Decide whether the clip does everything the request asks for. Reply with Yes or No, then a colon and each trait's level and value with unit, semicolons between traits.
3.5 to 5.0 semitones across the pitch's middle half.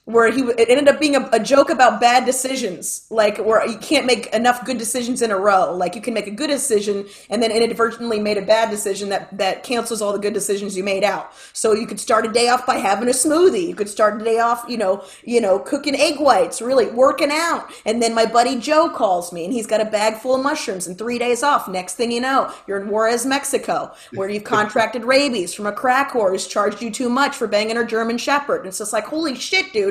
Yes: average, 3.9 semitones